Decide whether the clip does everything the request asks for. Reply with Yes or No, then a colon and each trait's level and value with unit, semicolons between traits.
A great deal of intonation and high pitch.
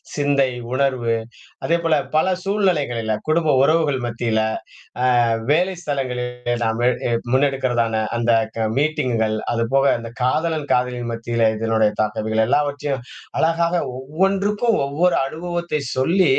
No: wide, 5.7 semitones; low, 135 Hz